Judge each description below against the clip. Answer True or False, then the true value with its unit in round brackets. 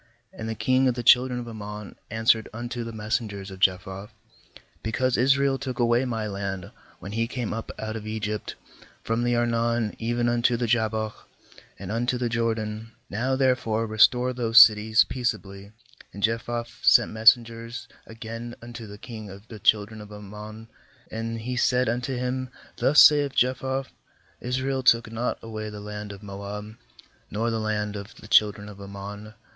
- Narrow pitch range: True (2.3 semitones)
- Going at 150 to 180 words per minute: True (170 wpm)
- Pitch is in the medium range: False (115 Hz)